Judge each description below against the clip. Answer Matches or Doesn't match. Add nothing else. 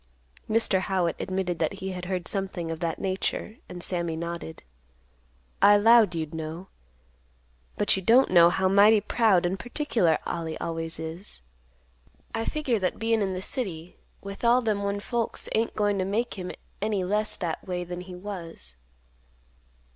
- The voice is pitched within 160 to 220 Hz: Matches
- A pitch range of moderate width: Matches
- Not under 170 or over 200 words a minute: Doesn't match